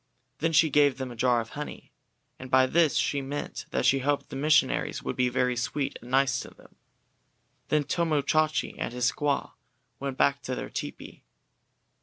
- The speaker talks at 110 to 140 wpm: No, average, 185 wpm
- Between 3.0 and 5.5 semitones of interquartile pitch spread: No, narrow, 2.5 semitones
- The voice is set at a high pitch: No, low, 135 Hz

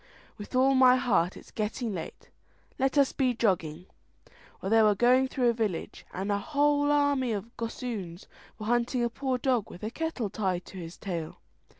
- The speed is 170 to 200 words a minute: Yes, average, 185 wpm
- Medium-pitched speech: No, high, 235 Hz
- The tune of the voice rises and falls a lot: No, average, 4.8 semitones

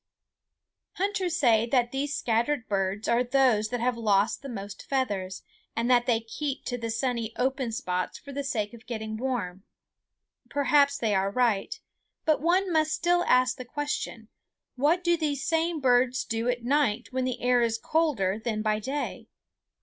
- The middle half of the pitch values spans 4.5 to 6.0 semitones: No, average, 4.1 semitones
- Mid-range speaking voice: No, high, 245 Hz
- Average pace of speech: Yes, average, 170 wpm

